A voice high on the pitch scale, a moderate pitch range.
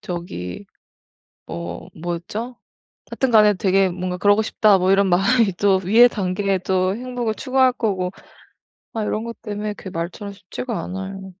Yes: high, 195 Hz; average, 3.1 semitones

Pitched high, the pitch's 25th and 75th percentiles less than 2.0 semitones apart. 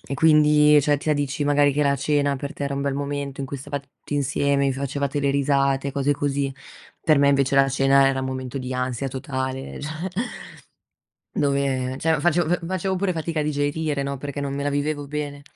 No: medium, 140 Hz; narrow, 1.2 semitones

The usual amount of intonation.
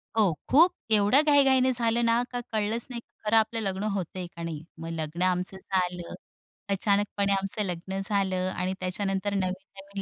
Yes: average, 3.2 semitones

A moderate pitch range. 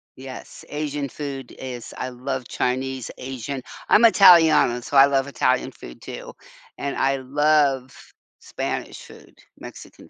No: narrow, 2.2 semitones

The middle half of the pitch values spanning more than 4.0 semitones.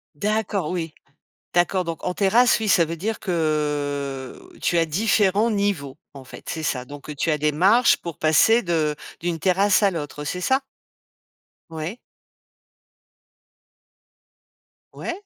Yes: average, 5.0 semitones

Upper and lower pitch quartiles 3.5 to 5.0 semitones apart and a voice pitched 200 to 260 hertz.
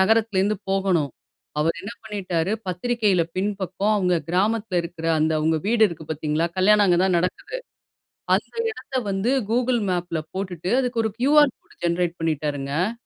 No: average, 4.2 semitones; high, 190 Hz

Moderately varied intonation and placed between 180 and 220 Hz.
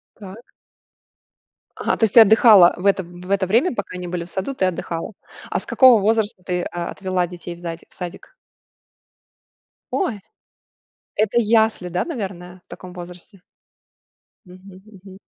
Yes: average, 3.5 semitones; high, 190 Hz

